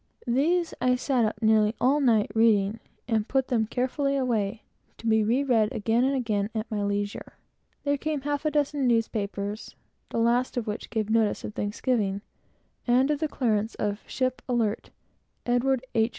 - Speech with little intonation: No, average, 3.5 semitones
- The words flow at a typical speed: Yes, average, 190 wpm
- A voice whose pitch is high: Yes, high, 230 Hz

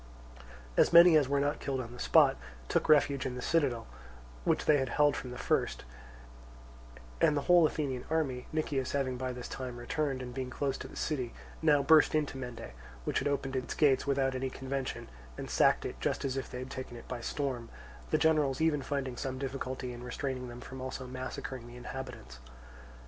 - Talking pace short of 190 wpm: No, average, 200 wpm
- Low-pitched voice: Yes, low, 130 Hz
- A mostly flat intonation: Yes, narrow, 2.2 semitones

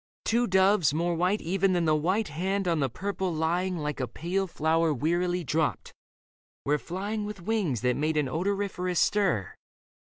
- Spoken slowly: No, average, 165 wpm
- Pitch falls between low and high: Yes, medium, 175 Hz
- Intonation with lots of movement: No, average, 3.8 semitones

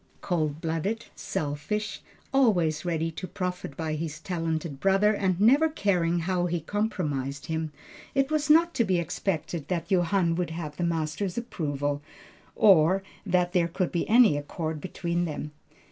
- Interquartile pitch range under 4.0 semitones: Yes, average, 3.6 semitones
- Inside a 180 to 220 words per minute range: No, average, 150 wpm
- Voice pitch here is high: No, medium, 175 Hz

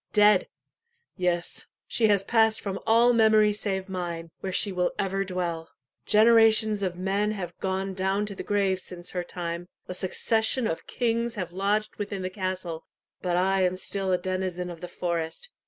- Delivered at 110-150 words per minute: No, average, 170 wpm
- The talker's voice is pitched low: No, high, 190 Hz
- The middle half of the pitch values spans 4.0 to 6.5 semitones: No, average, 2.7 semitones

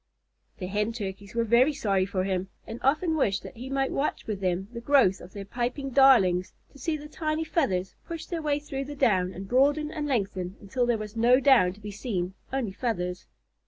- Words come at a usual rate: No, fast, 210 wpm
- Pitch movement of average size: No, wide, 6.2 semitones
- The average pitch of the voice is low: No, high, 230 Hz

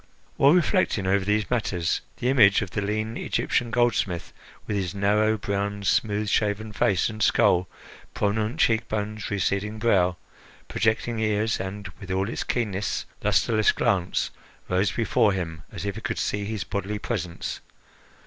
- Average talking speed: Yes, average, 150 wpm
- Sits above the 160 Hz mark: No, low, 105 Hz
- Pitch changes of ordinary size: No, narrow, 1.9 semitones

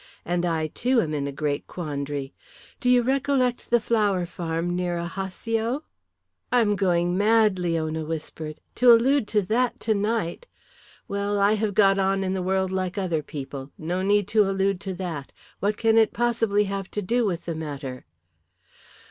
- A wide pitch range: No, average, 4.6 semitones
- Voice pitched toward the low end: No, high, 190 Hz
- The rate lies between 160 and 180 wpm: Yes, average, 170 wpm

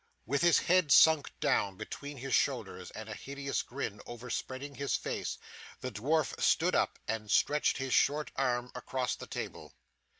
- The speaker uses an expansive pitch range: No, average, 3.2 semitones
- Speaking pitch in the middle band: No, low, 130 Hz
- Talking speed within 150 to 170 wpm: Yes, average, 165 wpm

